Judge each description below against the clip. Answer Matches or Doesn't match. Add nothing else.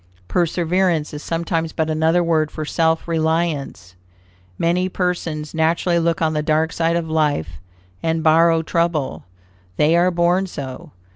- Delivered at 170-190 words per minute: Doesn't match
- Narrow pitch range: Matches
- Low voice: Doesn't match